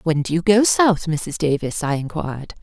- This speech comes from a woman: Yes, female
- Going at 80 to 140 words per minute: No, fast, 205 wpm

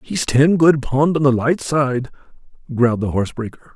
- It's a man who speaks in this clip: Yes, male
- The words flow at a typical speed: Yes, average, 190 wpm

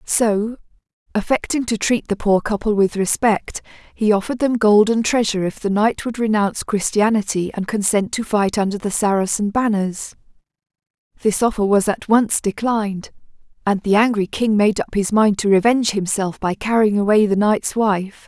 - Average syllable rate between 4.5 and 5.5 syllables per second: Yes, 5.0 syllables/s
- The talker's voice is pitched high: Yes, high, 210 Hz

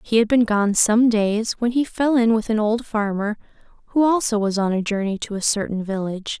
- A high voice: Yes, high, 220 Hz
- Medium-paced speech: No, fast, 225 wpm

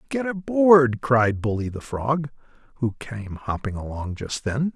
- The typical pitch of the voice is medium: No, low, 130 Hz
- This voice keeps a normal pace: Yes, average, 165 wpm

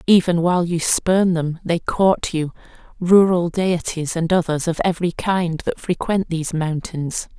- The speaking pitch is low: No, medium, 170 Hz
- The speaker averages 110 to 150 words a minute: Yes, average, 145 wpm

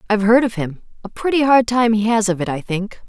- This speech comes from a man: No, female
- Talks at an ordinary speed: No, fast, 275 wpm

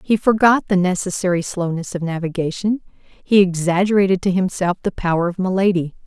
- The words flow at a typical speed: Yes, average, 150 wpm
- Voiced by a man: No, female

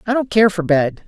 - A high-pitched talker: Yes, high, 200 Hz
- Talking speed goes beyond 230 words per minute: Yes, fast, 280 wpm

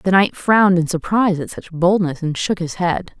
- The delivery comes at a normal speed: No, fast, 225 wpm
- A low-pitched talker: No, medium, 180 Hz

